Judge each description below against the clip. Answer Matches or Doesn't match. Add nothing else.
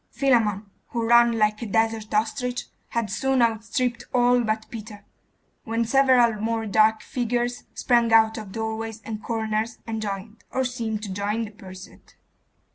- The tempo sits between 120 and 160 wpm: Matches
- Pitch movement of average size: Doesn't match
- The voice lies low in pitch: Doesn't match